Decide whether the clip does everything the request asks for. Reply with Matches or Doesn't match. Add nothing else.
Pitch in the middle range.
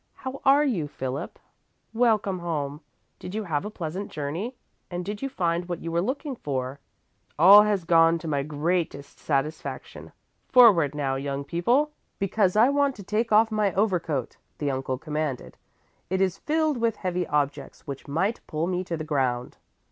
Matches